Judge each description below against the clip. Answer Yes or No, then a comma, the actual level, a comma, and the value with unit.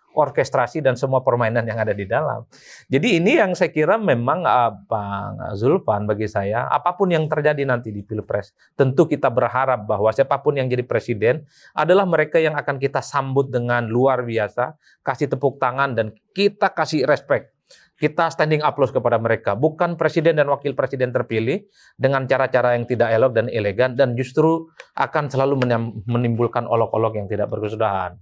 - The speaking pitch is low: Yes, low, 130 Hz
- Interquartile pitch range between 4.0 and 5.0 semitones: Yes, average, 4.5 semitones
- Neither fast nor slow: No, fast, 160 wpm